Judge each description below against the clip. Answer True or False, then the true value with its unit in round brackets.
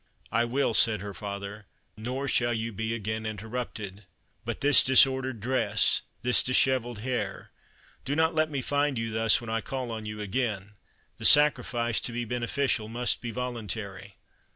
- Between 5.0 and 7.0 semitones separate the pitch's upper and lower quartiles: False (3.2 semitones)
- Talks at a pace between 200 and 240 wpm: False (160 wpm)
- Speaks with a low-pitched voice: True (115 Hz)